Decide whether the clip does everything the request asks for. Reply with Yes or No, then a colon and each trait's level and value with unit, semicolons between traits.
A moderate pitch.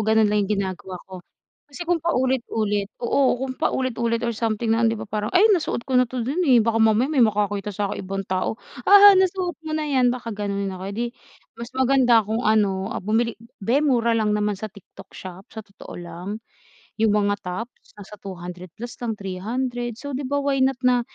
No: high, 225 Hz